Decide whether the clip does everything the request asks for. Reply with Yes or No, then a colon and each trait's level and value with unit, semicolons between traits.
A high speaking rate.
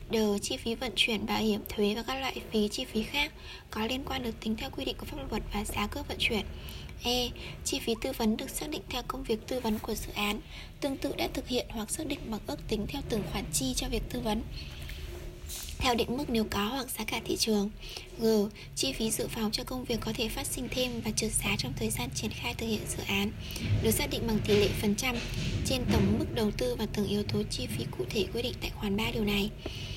Yes: fast, 260 wpm